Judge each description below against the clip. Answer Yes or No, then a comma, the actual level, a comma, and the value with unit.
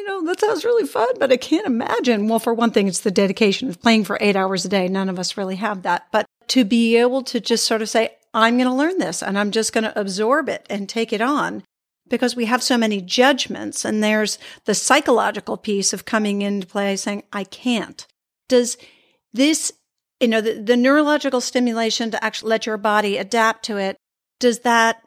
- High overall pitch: Yes, high, 225 Hz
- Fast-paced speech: Yes, fast, 215 wpm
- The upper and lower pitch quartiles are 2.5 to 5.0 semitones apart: Yes, average, 3.1 semitones